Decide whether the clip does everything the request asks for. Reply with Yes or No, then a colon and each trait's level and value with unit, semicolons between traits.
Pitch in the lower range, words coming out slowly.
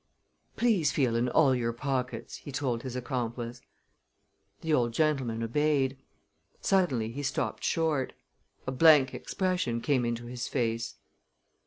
Yes: low, 130 Hz; slow, 130 wpm